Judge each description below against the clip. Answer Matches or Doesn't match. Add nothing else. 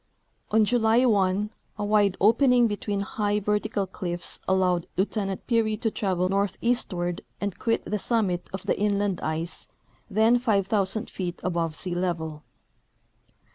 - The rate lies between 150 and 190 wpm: Doesn't match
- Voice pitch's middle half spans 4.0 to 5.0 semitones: Doesn't match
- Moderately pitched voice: Doesn't match